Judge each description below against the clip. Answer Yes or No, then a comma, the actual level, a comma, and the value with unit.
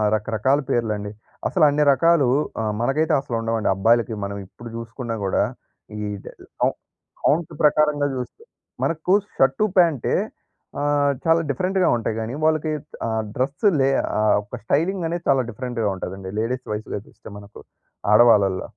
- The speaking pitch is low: Yes, low, 125 Hz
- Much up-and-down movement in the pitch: Yes, wide, 5.7 semitones